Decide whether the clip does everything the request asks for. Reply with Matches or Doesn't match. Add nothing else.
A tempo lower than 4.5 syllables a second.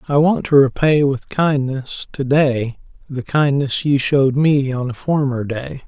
Matches